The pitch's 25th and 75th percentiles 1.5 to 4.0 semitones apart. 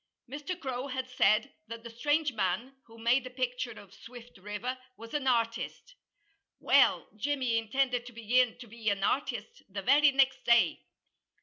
Yes: average, 2.7 semitones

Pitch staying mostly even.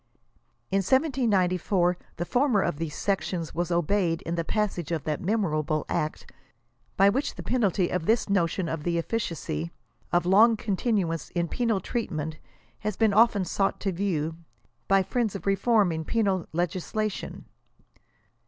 No: average, 4.2 semitones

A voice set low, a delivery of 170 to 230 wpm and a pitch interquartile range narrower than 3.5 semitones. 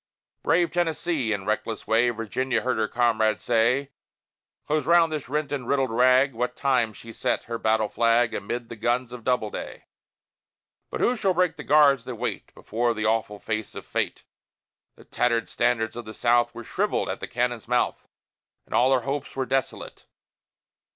Yes: low, 120 Hz; average, 175 wpm; average, 2.9 semitones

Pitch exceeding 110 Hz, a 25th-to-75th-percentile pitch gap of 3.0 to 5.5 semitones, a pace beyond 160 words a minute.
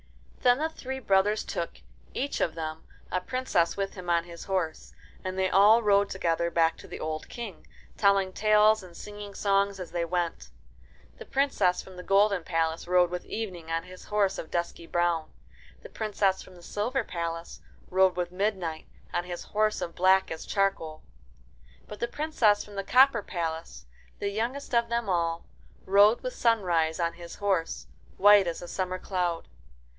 Yes: high, 190 Hz; average, 3.5 semitones; average, 175 wpm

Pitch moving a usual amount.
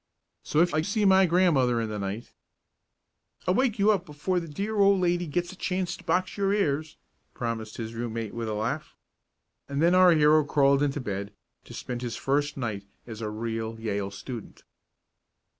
No: wide, 7.9 semitones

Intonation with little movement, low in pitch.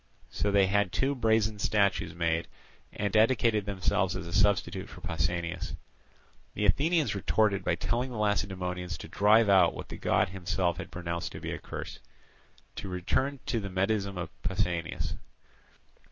No: average, 3.0 semitones; low, 100 Hz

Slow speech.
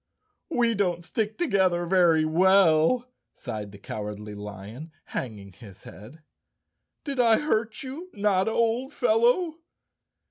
Yes: slow, 115 wpm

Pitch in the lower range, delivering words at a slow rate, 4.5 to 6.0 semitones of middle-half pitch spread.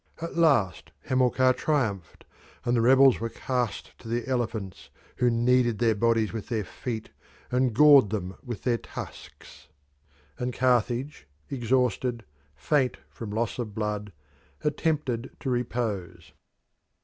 No: low, 120 Hz; slow, 125 wpm; average, 2.9 semitones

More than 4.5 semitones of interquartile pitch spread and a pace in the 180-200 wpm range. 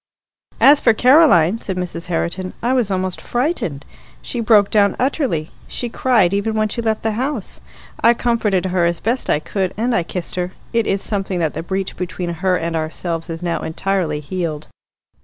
Yes: average, 5.0 semitones; average, 185 wpm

